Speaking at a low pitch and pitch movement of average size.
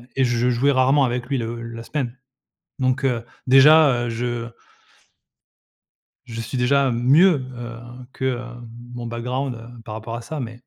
No: low, 125 Hz; narrow, 2.2 semitones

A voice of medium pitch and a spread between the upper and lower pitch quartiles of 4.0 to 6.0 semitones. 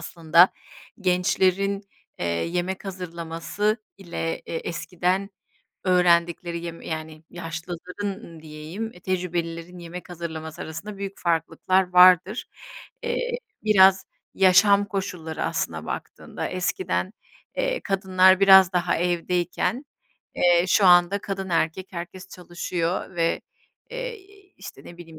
No: medium, 180 Hz; narrow, 2.4 semitones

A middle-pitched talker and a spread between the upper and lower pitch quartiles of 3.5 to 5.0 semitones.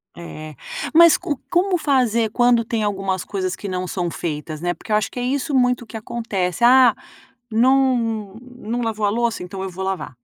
No: high, 225 Hz; average, 4.7 semitones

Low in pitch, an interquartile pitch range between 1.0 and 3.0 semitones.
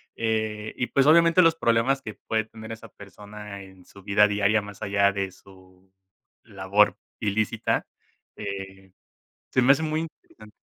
Yes: low, 105 Hz; narrow, 2.5 semitones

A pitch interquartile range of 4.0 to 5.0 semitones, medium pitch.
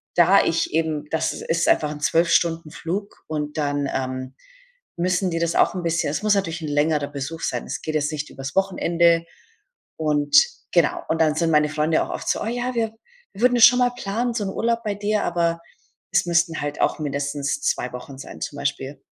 Yes: average, 4.5 semitones; medium, 165 Hz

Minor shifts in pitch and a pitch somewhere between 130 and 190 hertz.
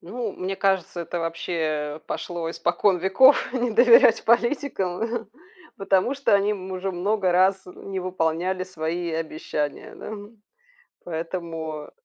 No: average, 3.3 semitones; medium, 185 Hz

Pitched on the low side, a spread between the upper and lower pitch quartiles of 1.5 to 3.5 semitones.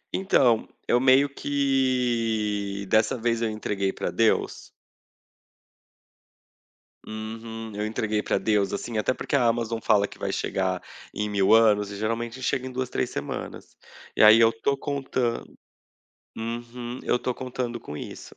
Yes: low, 115 Hz; average, 2.8 semitones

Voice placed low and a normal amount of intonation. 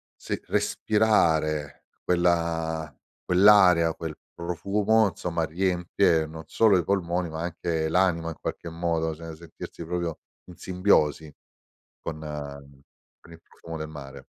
No: very low, 85 Hz; narrow, 2.0 semitones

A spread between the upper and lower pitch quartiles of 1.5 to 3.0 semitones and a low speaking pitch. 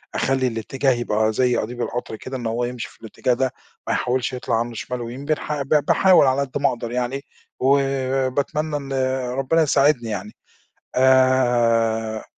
Yes: narrow, 2.5 semitones; low, 130 Hz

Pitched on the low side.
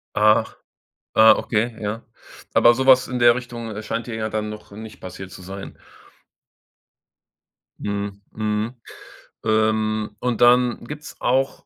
Yes: low, 110 Hz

